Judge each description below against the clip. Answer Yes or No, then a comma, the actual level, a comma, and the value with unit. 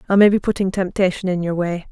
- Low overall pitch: No, medium, 185 Hz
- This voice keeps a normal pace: No, fast, 250 wpm